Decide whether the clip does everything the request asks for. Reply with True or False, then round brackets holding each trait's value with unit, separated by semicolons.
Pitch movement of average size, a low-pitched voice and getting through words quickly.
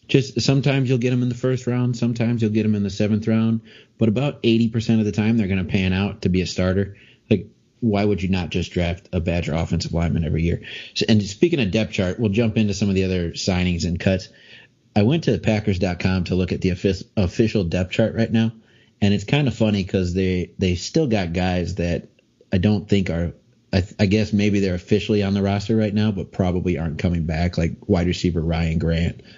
True (3.7 semitones; 100 Hz; 230 wpm)